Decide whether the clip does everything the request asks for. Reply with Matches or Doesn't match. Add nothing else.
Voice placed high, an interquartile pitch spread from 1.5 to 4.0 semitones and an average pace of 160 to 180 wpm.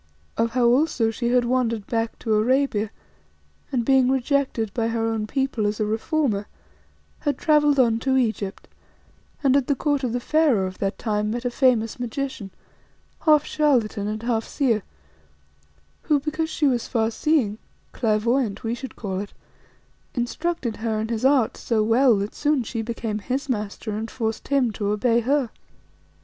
Matches